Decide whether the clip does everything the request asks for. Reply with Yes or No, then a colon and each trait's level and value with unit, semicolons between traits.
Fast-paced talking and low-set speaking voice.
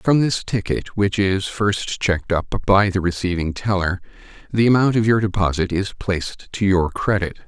No: average, 175 wpm; low, 100 Hz